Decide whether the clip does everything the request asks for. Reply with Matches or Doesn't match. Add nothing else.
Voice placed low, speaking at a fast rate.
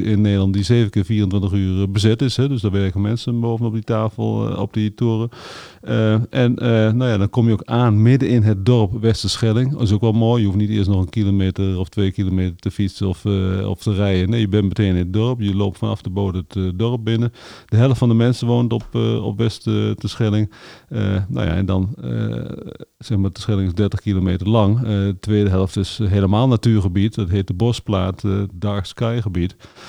Matches